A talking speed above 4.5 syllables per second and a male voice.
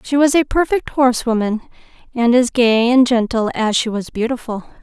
No: 5.2 syllables/s; female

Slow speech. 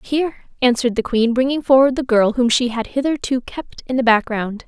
No: fast, 205 wpm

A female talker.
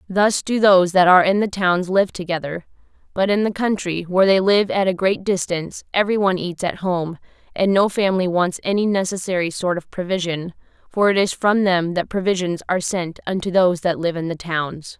Yes: female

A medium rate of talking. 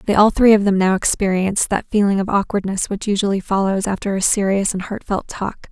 No: fast, 210 wpm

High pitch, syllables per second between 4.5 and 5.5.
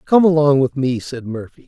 No: medium, 140 Hz; 5.2 syllables/s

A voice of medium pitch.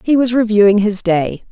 No: high, 215 Hz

